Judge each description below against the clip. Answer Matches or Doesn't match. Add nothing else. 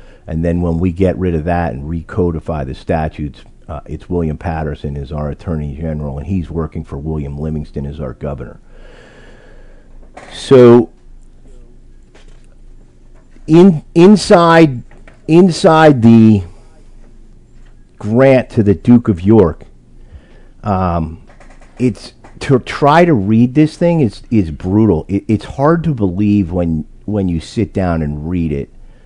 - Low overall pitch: Matches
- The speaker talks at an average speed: Doesn't match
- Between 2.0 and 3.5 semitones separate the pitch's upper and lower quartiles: Doesn't match